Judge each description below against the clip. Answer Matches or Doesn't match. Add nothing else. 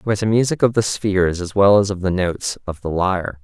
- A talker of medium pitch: Doesn't match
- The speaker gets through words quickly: Matches